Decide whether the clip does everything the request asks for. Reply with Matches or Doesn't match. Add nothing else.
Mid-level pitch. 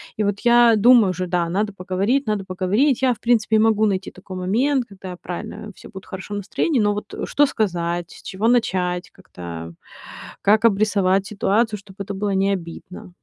Doesn't match